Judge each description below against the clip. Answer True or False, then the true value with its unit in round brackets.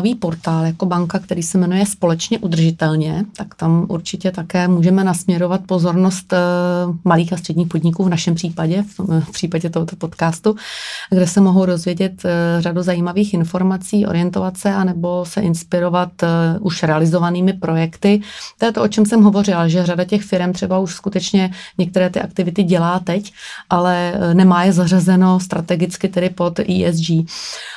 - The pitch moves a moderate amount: False (1.7 semitones)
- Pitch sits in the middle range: True (180 Hz)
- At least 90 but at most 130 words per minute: False (145 wpm)